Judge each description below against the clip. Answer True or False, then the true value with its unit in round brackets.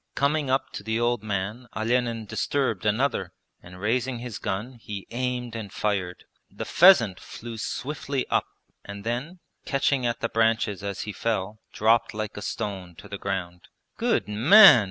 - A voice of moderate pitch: False (115 Hz)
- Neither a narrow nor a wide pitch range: True (3.8 semitones)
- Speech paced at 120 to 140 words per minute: False (160 wpm)